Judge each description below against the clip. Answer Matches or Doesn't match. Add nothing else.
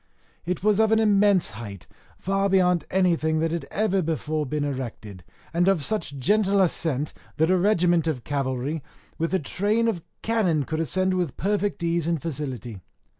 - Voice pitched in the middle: Matches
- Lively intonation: Doesn't match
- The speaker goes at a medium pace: Matches